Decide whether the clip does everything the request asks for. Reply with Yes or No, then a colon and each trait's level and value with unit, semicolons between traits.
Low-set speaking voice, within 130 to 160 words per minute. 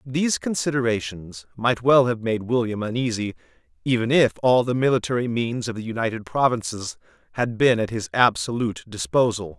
Yes: low, 115 Hz; average, 150 wpm